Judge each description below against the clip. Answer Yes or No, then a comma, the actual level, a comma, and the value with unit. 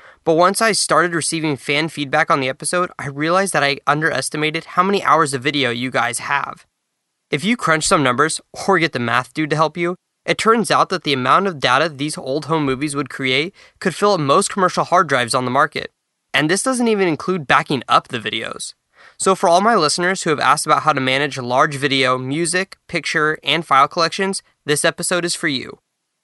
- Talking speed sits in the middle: No, fast, 215 wpm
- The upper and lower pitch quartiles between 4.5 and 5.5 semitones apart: No, average, 4.0 semitones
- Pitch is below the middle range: No, medium, 160 Hz